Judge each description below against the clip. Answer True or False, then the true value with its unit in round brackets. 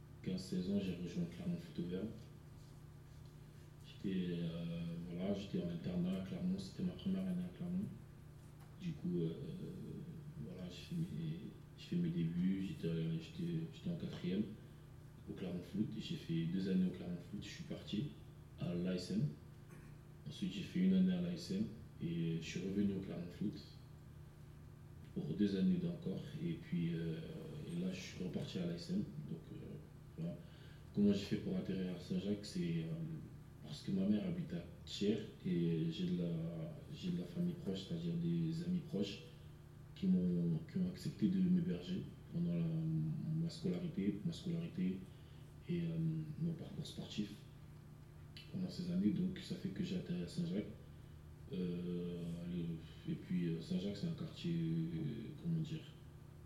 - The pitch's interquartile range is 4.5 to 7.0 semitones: False (4.0 semitones)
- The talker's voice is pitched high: False (165 Hz)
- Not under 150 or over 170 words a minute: True (155 wpm)